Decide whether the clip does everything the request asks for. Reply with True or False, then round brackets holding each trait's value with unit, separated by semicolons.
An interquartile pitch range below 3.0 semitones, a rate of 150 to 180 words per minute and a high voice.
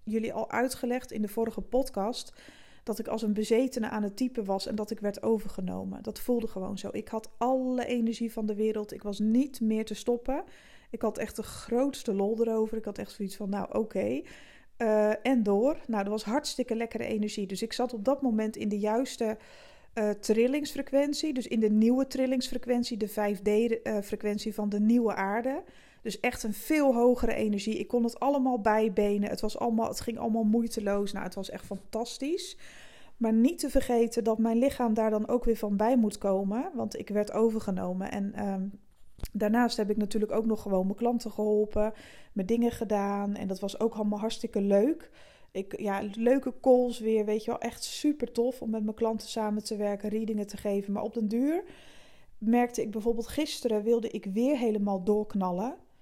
False (2.4 semitones; 195 wpm; 220 Hz)